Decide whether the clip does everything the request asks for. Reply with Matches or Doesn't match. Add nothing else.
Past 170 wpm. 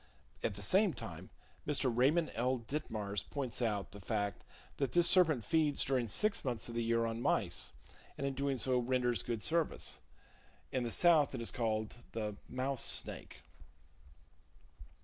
Doesn't match